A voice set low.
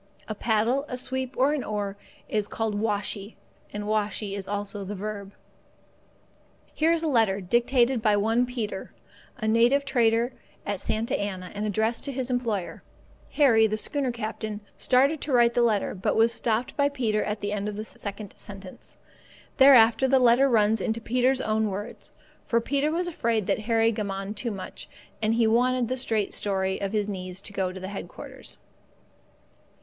No: high, 220 Hz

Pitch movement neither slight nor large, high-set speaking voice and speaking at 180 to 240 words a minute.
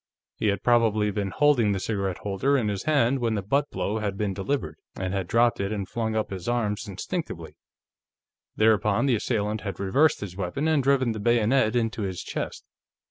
No: average, 3.4 semitones; low, 110 Hz; average, 190 wpm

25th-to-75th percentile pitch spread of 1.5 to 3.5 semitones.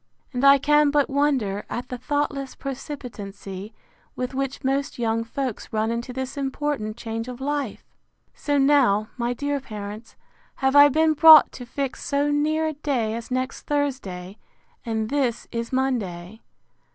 No: average, 4.1 semitones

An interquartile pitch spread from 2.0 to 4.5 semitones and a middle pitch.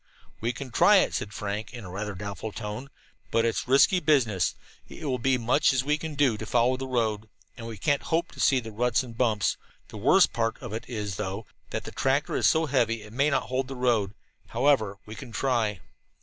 No: average, 3.9 semitones; low, 120 Hz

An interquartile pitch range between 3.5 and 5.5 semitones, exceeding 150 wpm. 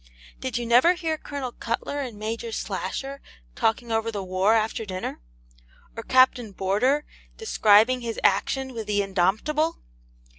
No: average, 4.0 semitones; average, 140 wpm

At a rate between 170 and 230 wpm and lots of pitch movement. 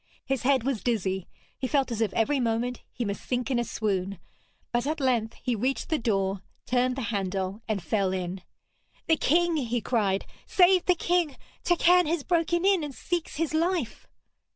Yes: average, 180 wpm; wide, 6.8 semitones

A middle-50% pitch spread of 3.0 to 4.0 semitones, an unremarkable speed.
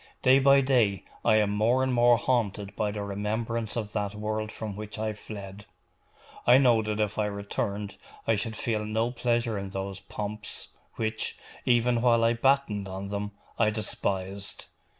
No: narrow, 2.4 semitones; average, 170 wpm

